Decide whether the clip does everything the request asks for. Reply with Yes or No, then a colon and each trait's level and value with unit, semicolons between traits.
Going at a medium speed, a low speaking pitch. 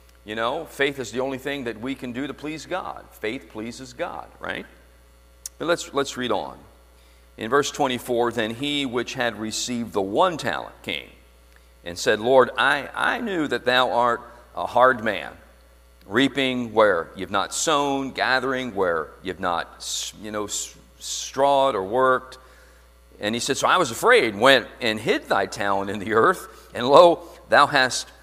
Yes: average, 170 wpm; low, 120 Hz